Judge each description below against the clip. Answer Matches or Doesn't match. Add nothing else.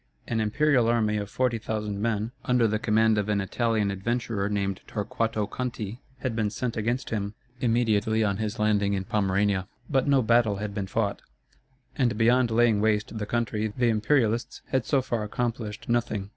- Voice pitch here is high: Doesn't match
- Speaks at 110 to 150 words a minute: Doesn't match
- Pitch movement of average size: Doesn't match